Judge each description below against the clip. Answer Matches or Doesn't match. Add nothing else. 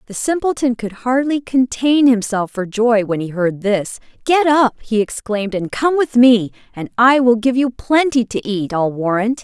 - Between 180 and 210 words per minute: Matches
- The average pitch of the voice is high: Matches